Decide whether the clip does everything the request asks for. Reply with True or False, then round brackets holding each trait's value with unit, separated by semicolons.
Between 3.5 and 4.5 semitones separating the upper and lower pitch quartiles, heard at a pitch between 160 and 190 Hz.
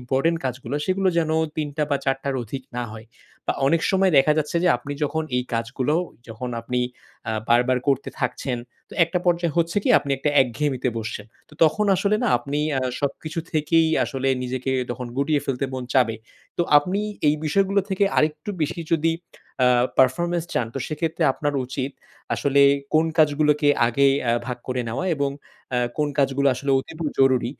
False (3.8 semitones; 140 Hz)